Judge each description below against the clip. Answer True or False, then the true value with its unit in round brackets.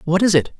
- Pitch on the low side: False (180 Hz)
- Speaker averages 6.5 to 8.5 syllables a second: True (6.8 syllables/s)